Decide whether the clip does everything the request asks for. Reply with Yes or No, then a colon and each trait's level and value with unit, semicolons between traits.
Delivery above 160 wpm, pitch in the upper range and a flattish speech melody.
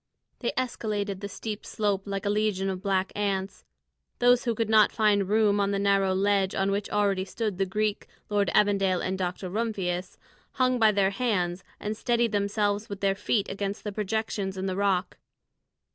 Yes: average, 180 wpm; high, 200 Hz; narrow, 1.7 semitones